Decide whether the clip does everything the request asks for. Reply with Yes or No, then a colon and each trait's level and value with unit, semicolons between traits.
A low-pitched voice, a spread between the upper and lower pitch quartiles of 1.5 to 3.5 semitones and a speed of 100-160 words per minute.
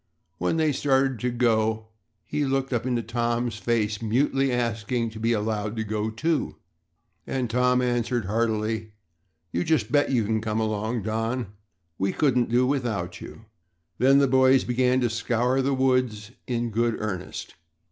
Yes: low, 120 Hz; average, 2.7 semitones; average, 155 wpm